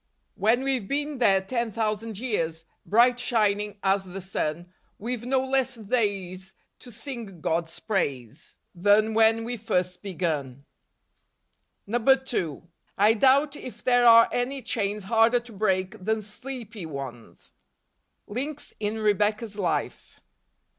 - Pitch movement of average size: Yes, average, 4.2 semitones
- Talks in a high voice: Yes, high, 215 Hz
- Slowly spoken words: Yes, slow, 125 wpm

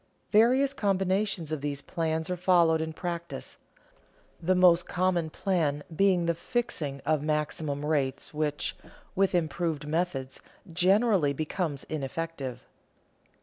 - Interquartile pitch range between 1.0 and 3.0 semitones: No, average, 3.6 semitones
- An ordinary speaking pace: No, slow, 115 wpm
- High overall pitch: No, medium, 165 Hz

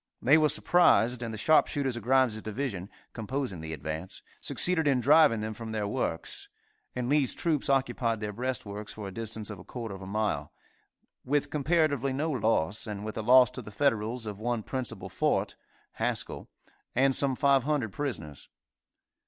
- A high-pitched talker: No, low, 120 Hz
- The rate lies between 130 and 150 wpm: No, average, 170 wpm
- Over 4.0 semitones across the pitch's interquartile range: Yes, average, 4.5 semitones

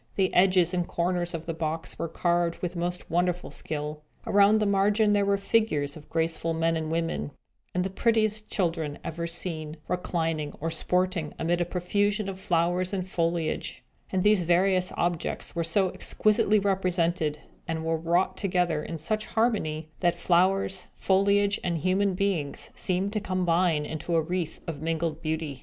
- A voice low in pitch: No, medium, 175 Hz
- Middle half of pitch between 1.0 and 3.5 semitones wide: Yes, average, 2.8 semitones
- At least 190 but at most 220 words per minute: No, average, 165 wpm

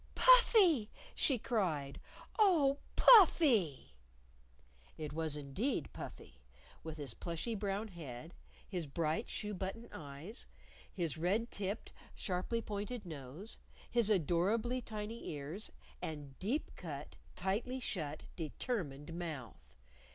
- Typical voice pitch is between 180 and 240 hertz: Yes, medium, 185 Hz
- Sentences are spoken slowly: Yes, slow, 105 wpm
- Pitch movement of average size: No, wide, 6.9 semitones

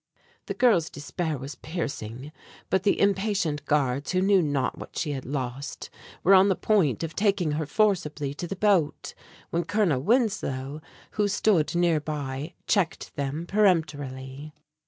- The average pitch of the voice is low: No, medium, 160 Hz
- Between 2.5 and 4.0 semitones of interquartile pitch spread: No, average, 5.3 semitones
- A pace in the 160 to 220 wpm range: No, average, 150 wpm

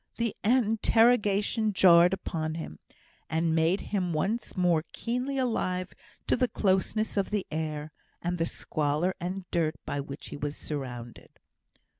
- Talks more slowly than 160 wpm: Yes, average, 140 wpm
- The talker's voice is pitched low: No, medium, 180 Hz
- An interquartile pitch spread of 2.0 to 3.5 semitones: No, average, 5.1 semitones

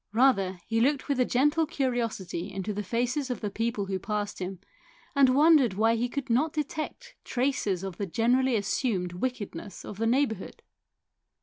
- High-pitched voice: Yes, high, 230 Hz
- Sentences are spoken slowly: No, average, 170 wpm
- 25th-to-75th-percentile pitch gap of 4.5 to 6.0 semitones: Yes, average, 4.8 semitones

